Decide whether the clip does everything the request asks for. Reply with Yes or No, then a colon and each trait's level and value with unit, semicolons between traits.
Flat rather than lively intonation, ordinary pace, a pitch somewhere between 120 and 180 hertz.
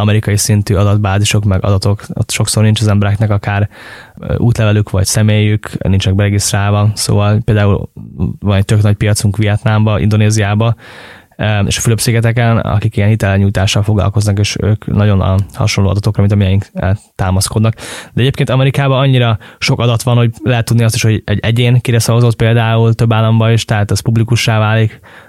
No: narrow, 2.0 semitones; average, 155 wpm; low, 105 Hz